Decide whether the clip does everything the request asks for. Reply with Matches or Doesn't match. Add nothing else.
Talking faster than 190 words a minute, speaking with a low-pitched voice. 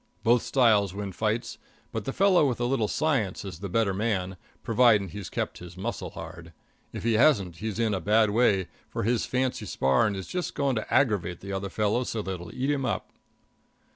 Matches